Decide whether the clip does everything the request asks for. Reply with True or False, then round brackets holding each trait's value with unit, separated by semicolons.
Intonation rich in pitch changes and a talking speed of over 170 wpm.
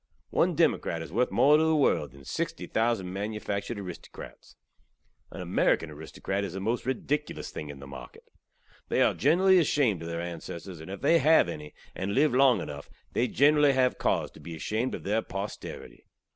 True (8.0 semitones; 180 wpm)